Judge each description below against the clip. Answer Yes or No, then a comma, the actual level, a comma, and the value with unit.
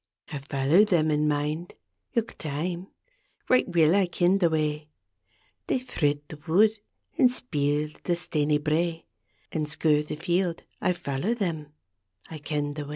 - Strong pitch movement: No, average, 3.1 semitones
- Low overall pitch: No, medium, 160 Hz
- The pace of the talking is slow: No, average, 160 wpm